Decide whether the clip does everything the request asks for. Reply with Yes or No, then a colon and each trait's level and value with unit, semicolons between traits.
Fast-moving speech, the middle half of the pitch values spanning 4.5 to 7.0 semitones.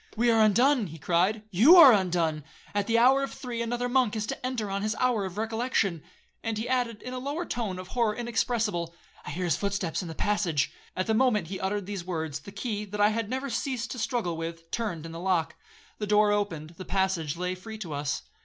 Yes: fast, 230 wpm; average, 4.8 semitones